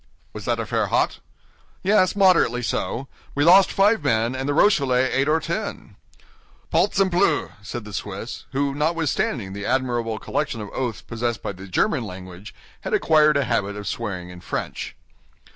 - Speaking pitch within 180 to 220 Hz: No, low, 130 Hz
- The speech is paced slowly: No, average, 160 wpm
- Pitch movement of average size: No, wide, 7.2 semitones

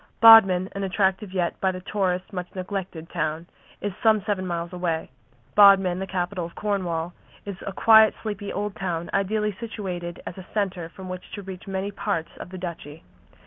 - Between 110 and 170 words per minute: No, average, 180 wpm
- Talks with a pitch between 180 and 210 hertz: Yes, high, 190 Hz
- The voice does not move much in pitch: Yes, narrow, 2.3 semitones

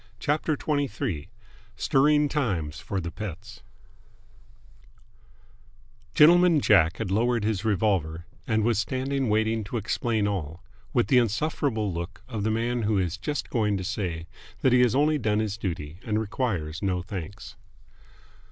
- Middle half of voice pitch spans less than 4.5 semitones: No, average, 4.8 semitones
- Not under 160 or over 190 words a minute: No, average, 145 wpm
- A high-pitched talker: No, low, 110 Hz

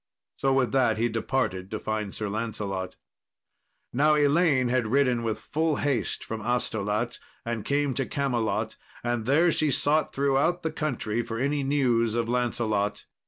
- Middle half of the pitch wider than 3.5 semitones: Yes, average, 4.2 semitones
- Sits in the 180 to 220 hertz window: No, low, 120 Hz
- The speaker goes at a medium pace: Yes, average, 155 wpm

